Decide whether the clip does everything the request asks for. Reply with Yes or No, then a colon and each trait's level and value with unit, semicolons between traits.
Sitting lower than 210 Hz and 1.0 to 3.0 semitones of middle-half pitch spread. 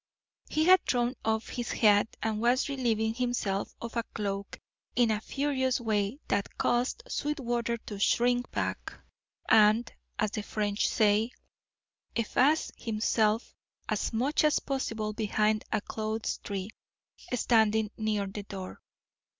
No: high, 225 Hz; narrow, 2.5 semitones